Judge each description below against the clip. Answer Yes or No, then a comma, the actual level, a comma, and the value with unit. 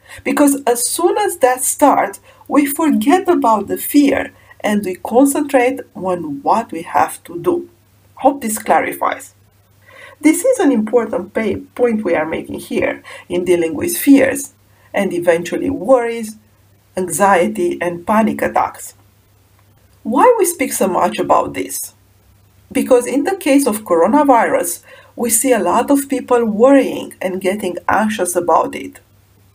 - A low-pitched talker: No, high, 230 Hz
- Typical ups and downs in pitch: No, wide, 8.1 semitones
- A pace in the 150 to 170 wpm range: No, average, 140 wpm